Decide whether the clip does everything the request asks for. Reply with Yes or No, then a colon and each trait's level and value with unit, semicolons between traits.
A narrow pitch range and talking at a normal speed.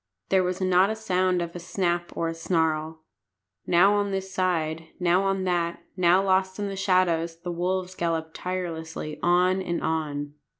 Yes: narrow, 2.2 semitones; average, 170 wpm